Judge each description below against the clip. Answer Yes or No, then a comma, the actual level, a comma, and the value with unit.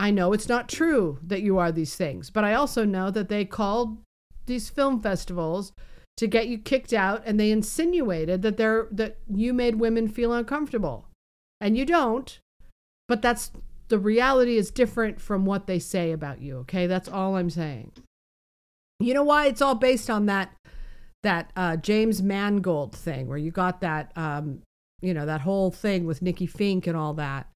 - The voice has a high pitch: Yes, high, 200 Hz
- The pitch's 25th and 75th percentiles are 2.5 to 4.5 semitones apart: No, average, 5.0 semitones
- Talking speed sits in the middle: Yes, average, 185 wpm